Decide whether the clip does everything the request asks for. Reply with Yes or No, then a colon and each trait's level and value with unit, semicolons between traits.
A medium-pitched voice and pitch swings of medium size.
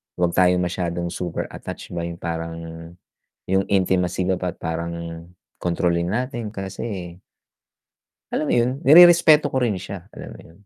No: very low, 90 Hz; average, 3.1 semitones